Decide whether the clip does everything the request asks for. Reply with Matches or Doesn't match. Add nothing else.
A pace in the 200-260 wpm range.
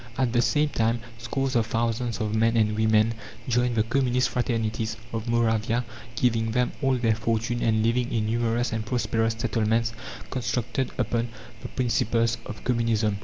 Doesn't match